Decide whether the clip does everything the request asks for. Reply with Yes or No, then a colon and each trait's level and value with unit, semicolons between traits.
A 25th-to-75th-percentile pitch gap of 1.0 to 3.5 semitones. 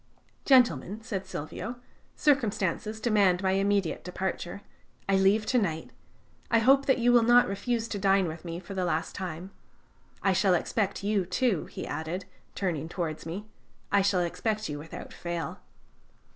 No: average, 3.9 semitones